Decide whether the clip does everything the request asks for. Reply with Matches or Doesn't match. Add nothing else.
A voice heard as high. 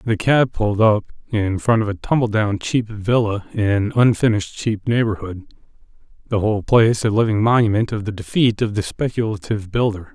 Doesn't match